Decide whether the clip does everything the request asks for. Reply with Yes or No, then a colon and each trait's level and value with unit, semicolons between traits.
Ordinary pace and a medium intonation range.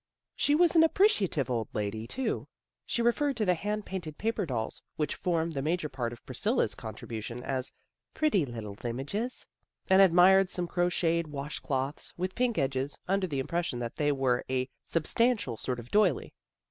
No: average, 180 wpm; wide, 7.2 semitones